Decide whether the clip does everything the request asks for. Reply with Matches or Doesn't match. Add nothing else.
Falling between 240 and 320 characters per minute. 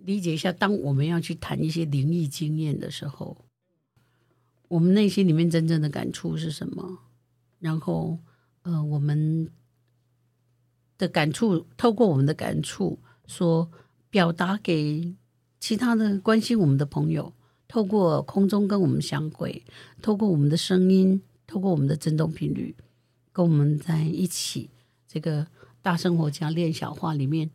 Doesn't match